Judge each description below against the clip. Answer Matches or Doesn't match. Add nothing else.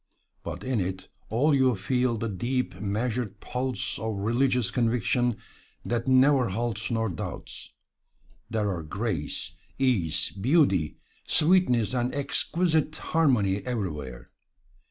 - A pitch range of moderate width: Matches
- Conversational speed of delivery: Doesn't match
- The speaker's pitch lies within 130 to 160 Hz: Doesn't match